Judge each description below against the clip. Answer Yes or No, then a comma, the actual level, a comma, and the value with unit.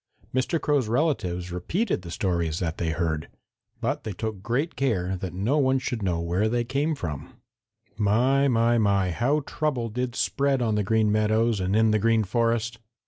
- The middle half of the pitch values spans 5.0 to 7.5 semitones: Yes, wide, 5.5 semitones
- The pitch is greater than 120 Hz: No, low, 110 Hz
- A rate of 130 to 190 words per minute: Yes, average, 180 wpm